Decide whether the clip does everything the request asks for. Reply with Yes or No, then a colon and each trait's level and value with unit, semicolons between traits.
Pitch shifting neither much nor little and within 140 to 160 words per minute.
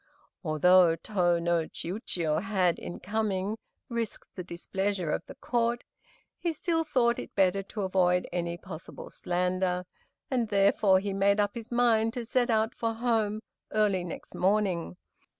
Yes: average, 3.8 semitones; average, 150 wpm